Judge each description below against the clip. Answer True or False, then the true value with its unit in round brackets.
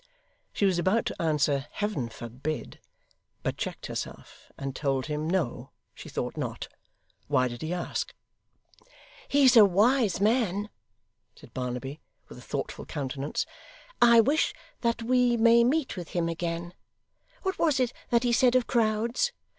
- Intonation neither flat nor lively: False (8.0 semitones)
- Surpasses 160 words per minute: False (145 wpm)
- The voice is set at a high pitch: True (195 Hz)